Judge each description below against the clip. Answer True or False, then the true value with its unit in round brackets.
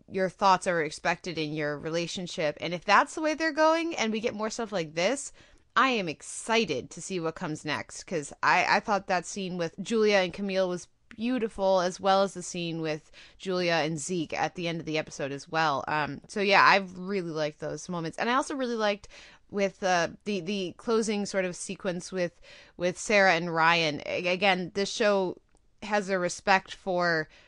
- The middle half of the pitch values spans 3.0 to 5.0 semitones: True (3.5 semitones)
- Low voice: False (185 Hz)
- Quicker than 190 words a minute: True (200 wpm)